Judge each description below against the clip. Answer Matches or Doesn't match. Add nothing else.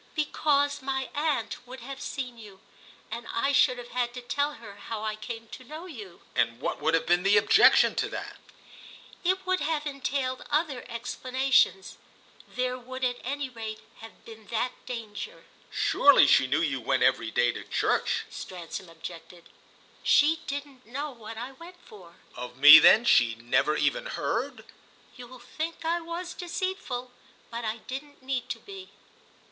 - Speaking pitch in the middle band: Doesn't match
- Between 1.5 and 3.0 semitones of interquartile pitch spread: Doesn't match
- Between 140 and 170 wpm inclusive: Matches